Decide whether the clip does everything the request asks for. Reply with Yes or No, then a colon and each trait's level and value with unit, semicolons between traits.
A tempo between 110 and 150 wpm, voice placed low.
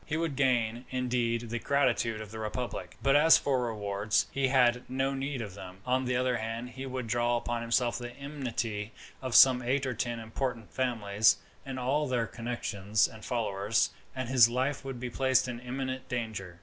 No: average, 190 wpm; low, 120 Hz